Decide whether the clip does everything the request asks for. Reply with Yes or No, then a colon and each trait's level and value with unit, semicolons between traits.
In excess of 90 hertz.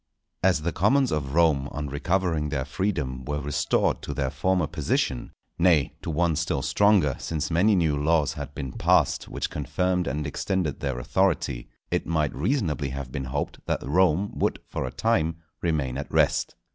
No: very low, 75 Hz